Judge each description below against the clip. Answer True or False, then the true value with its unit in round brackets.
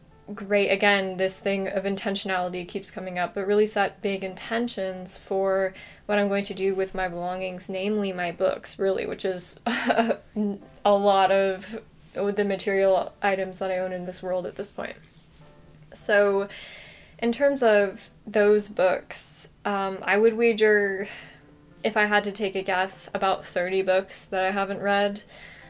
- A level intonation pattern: True (1.4 semitones)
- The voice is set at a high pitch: True (195 Hz)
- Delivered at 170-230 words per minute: False (160 wpm)